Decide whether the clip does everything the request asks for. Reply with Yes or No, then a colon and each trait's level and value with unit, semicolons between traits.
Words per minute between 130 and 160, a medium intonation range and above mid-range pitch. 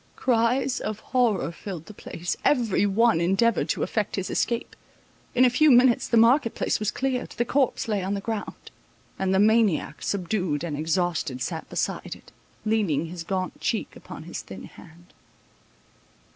Yes: average, 155 wpm; average, 4.9 semitones; high, 210 Hz